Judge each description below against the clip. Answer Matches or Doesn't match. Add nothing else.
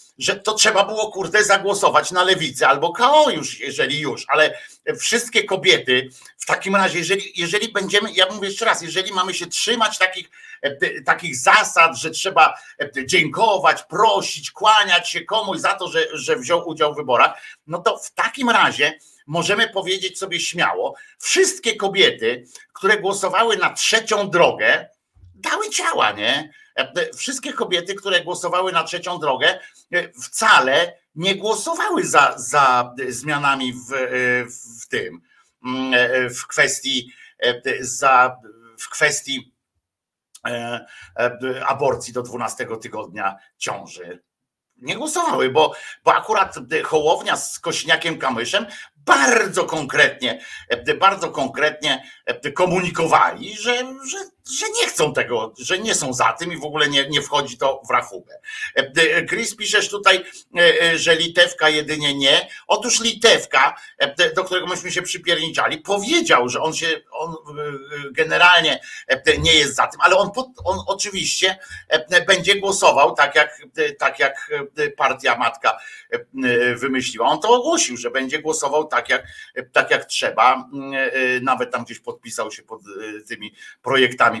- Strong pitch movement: Matches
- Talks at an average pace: Matches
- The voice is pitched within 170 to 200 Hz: Matches